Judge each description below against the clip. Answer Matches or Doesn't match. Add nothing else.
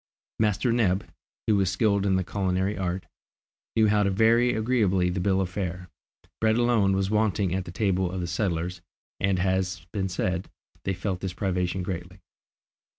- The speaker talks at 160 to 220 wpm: Matches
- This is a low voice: Matches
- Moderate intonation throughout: Doesn't match